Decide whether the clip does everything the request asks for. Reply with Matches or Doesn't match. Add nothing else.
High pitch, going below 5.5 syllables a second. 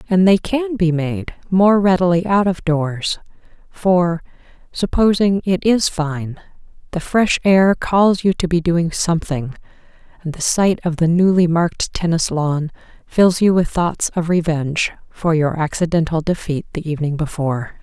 Doesn't match